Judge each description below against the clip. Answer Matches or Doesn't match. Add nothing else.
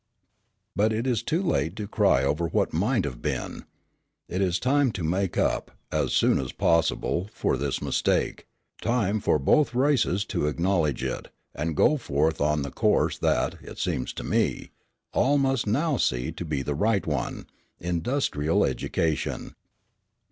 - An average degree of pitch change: Doesn't match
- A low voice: Matches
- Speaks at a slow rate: Doesn't match